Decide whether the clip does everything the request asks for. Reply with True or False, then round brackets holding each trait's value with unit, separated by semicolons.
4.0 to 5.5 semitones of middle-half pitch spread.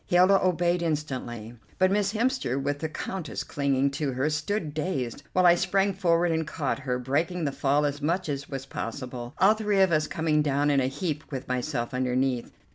True (4.7 semitones)